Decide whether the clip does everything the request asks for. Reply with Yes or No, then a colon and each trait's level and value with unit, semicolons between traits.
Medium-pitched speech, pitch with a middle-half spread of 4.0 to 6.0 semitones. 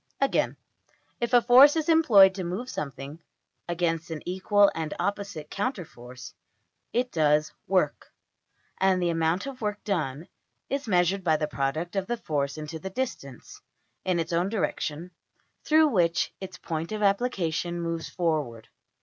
Yes: medium, 175 Hz; average, 4.5 semitones